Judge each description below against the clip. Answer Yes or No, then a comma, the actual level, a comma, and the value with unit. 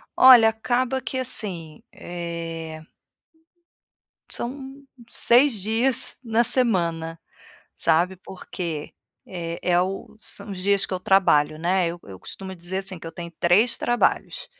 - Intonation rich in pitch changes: Yes, wide, 5.8 semitones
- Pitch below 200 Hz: Yes, high, 190 Hz